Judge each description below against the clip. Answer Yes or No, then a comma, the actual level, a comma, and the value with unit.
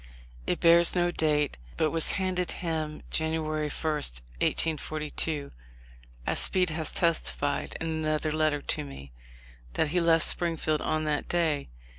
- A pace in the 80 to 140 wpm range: Yes, slow, 135 wpm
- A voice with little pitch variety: Yes, narrow, 1.7 semitones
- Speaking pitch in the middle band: Yes, medium, 155 Hz